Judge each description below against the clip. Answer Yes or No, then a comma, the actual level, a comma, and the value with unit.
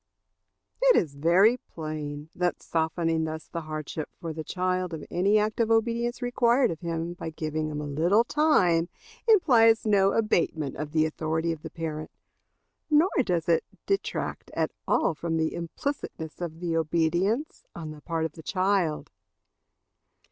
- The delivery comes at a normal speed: Yes, average, 155 wpm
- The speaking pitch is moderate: Yes, medium, 170 Hz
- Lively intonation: No, average, 5.0 semitones